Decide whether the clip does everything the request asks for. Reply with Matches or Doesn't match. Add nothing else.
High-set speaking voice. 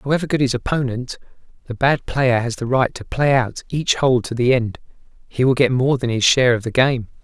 Doesn't match